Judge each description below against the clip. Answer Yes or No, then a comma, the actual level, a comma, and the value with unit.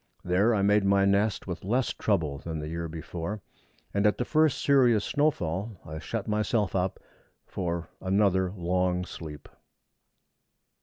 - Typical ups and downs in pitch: Yes, average, 3.7 semitones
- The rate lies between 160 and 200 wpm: No, average, 145 wpm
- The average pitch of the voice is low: Yes, very low, 95 Hz